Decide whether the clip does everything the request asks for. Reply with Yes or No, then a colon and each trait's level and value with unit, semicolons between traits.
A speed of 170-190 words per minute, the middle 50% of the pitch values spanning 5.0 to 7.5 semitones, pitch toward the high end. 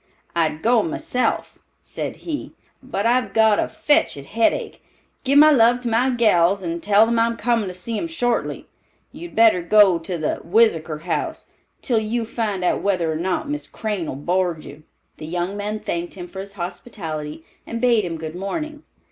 Yes: average, 180 wpm; average, 5.3 semitones; high, 205 Hz